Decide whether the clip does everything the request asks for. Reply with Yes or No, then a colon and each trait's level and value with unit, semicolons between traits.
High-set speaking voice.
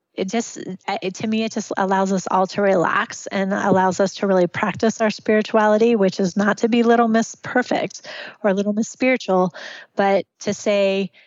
Yes: high, 205 Hz